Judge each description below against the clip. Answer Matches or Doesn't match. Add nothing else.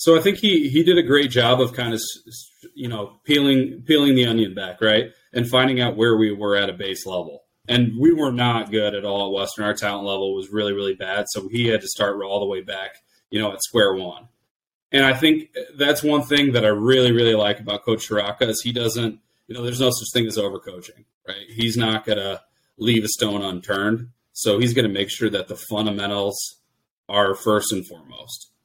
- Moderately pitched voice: Doesn't match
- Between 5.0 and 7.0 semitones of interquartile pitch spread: Doesn't match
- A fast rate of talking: Matches